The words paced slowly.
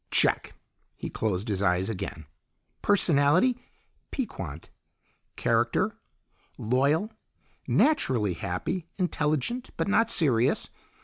Yes: slow, 85 wpm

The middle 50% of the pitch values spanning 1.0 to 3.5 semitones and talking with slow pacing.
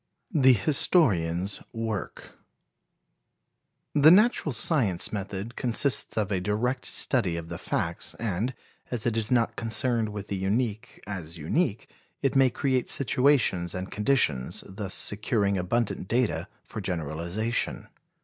No: average, 4.9 semitones; slow, 125 wpm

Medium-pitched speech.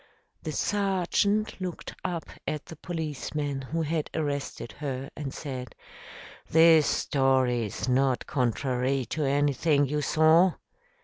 Yes: medium, 145 Hz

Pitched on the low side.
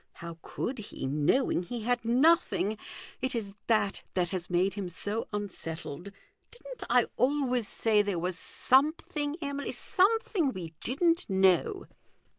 No: high, 220 Hz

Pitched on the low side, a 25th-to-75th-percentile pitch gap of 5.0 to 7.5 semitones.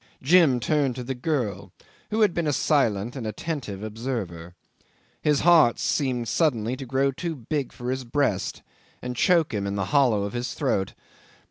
Yes: low, 125 Hz; average, 5.3 semitones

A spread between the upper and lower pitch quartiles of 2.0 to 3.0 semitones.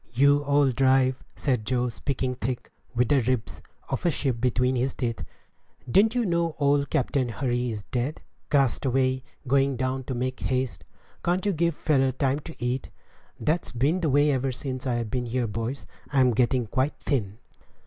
Yes: narrow, 2.4 semitones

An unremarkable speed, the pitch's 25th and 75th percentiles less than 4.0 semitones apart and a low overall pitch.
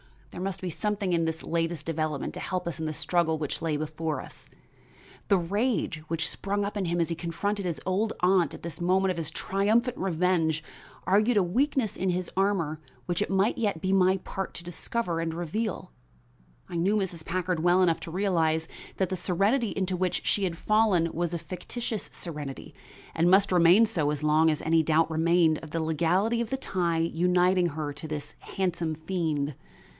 No: average, 195 wpm; average, 3.1 semitones; medium, 175 Hz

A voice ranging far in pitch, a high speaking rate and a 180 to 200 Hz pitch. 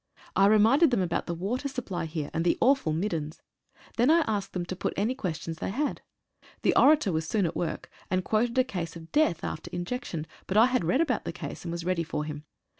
Yes: wide, 6.9 semitones; fast, 225 wpm; medium, 185 Hz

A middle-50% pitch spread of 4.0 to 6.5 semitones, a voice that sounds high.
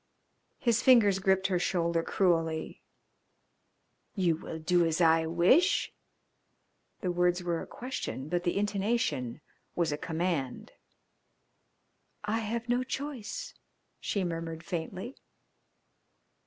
No: average, 4.3 semitones; medium, 180 Hz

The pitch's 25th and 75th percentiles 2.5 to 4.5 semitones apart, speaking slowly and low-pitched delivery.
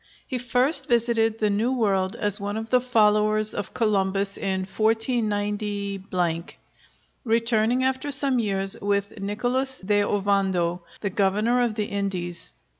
No: average, 2.9 semitones; slow, 130 wpm; high, 210 Hz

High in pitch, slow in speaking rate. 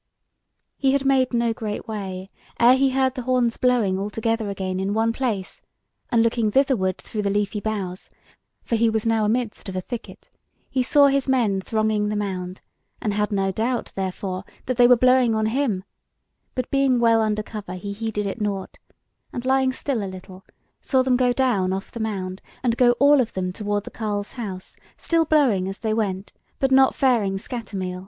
No: high, 220 Hz; average, 195 wpm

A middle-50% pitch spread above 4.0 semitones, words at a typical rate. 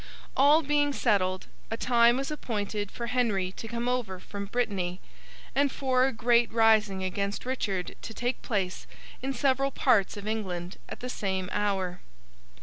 Yes: average, 4.4 semitones; average, 155 wpm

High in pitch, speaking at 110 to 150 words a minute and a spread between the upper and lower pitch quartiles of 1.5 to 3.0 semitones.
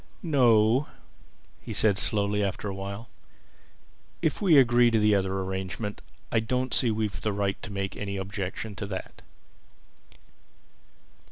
No: low, 105 Hz; average, 145 wpm; average, 2.7 semitones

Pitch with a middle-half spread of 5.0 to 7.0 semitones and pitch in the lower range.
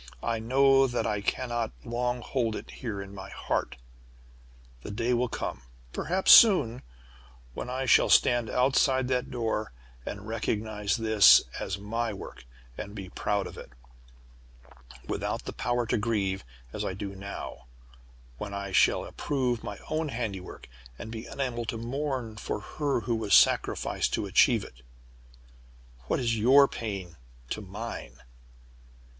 No: average, 3.6 semitones; low, 115 Hz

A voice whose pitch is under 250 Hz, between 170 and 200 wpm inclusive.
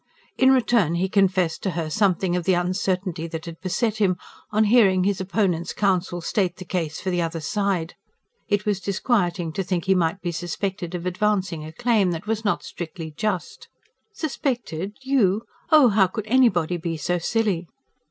Yes: medium, 185 Hz; average, 175 wpm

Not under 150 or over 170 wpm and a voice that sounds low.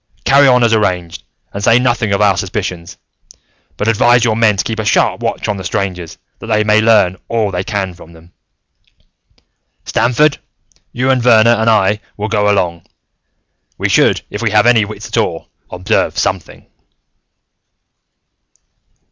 Yes: average, 160 wpm; low, 105 Hz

